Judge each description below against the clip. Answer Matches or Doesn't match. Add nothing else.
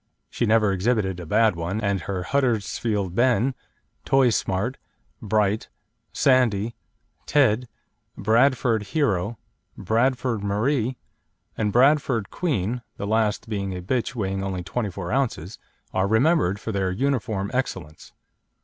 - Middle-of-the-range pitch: Doesn't match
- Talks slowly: Matches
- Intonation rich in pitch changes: Doesn't match